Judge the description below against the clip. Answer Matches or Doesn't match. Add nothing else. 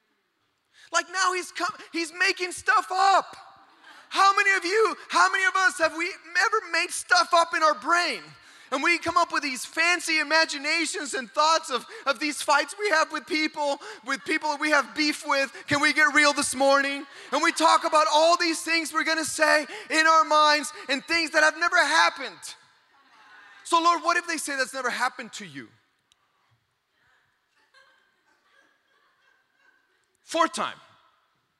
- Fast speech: Doesn't match